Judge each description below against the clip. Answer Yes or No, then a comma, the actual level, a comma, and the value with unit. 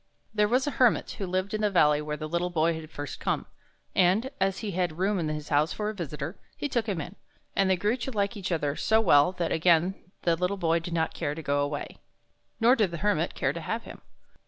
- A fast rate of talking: Yes, fast, 250 wpm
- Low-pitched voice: No, medium, 180 Hz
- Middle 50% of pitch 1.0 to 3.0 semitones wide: No, average, 4.6 semitones